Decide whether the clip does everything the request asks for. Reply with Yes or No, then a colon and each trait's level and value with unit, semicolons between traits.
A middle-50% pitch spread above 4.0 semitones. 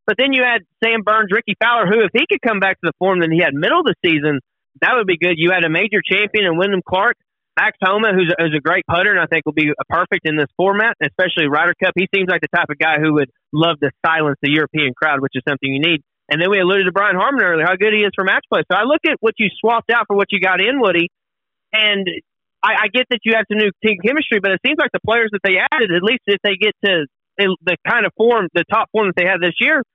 Yes: average, 4.5 semitones